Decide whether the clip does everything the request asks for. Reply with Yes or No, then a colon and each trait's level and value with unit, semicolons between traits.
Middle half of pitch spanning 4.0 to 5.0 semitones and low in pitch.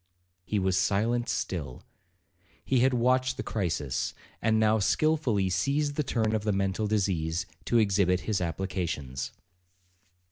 Yes: average, 4.6 semitones; low, 105 Hz